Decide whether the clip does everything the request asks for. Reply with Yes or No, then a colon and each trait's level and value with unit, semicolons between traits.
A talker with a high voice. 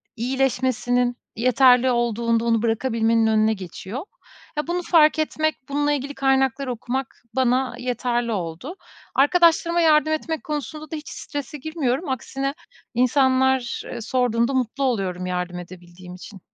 Yes: very high, 255 Hz